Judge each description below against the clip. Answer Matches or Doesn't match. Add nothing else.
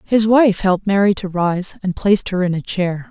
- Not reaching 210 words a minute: Doesn't match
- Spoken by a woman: Matches